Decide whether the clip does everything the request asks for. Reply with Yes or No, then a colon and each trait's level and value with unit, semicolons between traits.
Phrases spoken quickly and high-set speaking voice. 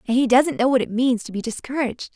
Yes: fast, 280 wpm; very high, 250 Hz